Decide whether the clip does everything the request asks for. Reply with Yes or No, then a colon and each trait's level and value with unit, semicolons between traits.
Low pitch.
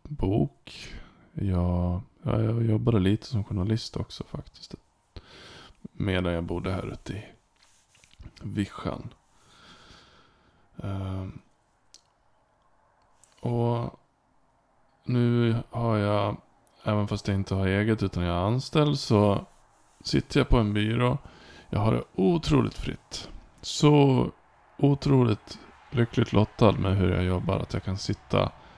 Yes: low, 105 Hz